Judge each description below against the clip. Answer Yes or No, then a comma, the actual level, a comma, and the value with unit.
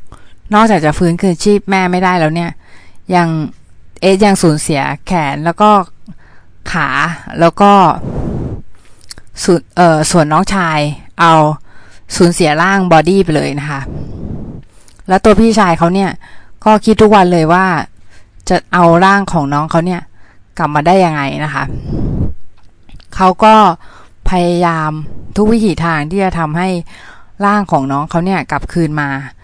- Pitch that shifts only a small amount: No, average, 5.3 semitones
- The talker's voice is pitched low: No, medium, 170 Hz